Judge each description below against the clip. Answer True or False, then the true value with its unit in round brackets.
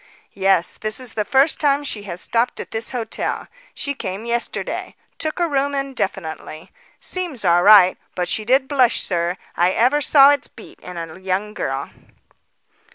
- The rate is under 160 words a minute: False (165 wpm)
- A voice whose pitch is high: True (220 Hz)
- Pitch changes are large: True (6.8 semitones)